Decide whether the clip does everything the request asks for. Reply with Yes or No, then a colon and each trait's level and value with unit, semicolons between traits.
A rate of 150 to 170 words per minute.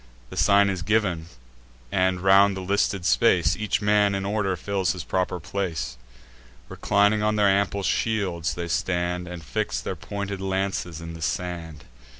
Yes: average, 155 wpm